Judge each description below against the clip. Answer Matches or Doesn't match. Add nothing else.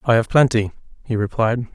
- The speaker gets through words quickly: Doesn't match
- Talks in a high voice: Doesn't match